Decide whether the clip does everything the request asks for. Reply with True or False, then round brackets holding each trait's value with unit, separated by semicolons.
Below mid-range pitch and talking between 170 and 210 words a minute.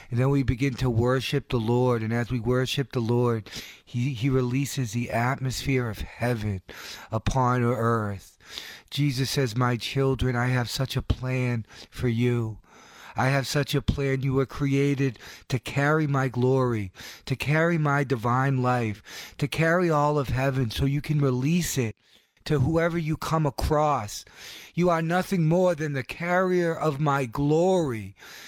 False (130 Hz; 160 wpm)